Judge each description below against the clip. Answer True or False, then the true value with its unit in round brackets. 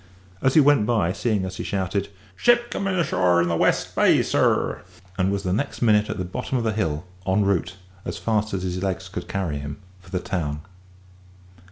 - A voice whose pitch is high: False (95 Hz)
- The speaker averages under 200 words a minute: False (205 wpm)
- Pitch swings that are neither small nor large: True (3.5 semitones)